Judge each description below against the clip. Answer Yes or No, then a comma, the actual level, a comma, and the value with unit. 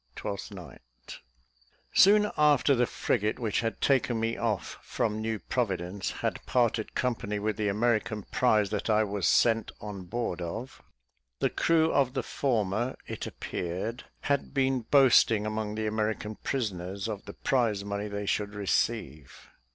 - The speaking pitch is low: Yes, low, 110 Hz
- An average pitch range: Yes, average, 3.1 semitones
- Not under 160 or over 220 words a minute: No, average, 150 wpm